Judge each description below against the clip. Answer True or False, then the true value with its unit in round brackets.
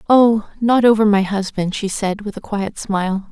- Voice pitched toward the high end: True (205 Hz)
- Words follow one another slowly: False (200 wpm)